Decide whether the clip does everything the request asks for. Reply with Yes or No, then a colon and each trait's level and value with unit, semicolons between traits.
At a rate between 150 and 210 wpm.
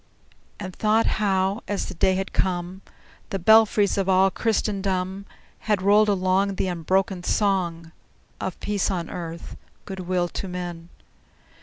No: average, 140 wpm